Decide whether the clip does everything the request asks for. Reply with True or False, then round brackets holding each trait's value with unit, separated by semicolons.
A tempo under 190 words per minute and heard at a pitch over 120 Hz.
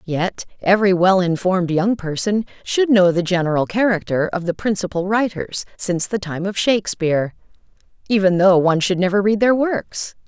True (165 wpm; 190 Hz)